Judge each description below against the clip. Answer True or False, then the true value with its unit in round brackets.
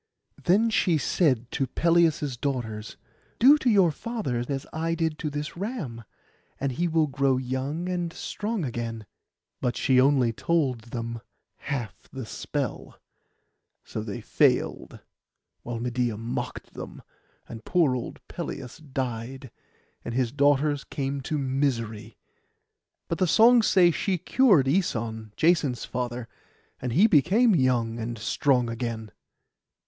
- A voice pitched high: False (135 Hz)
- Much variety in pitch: True (5.8 semitones)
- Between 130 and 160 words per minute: True (135 wpm)